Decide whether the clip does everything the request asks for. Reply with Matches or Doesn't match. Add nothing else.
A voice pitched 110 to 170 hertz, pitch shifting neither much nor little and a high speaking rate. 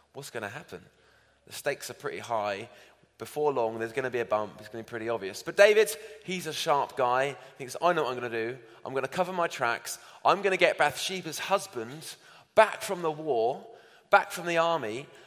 Doesn't match